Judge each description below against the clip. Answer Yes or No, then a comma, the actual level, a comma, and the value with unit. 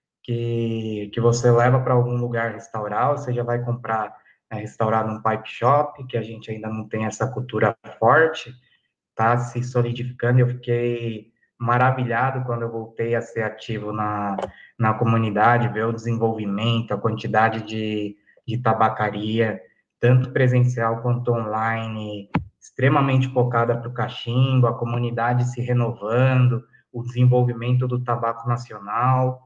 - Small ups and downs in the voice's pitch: Yes, narrow, 1.8 semitones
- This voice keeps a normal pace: Yes, average, 135 wpm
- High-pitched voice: No, low, 120 Hz